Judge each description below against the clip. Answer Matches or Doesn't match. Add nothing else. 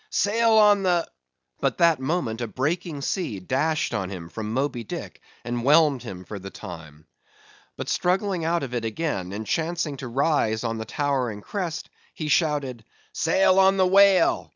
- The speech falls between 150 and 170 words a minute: Matches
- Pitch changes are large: Matches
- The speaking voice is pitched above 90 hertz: Matches